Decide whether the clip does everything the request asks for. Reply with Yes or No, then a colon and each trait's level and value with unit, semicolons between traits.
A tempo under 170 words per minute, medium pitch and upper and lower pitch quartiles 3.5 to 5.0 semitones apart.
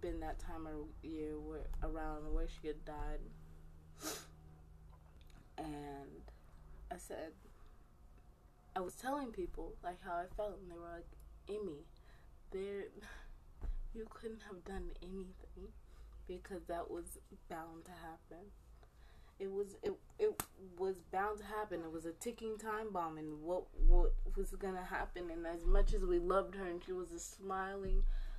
Yes: average, 150 wpm; medium, 175 Hz; average, 4.7 semitones